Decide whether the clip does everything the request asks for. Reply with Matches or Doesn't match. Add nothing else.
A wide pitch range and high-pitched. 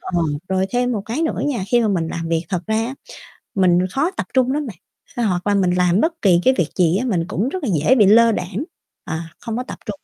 Matches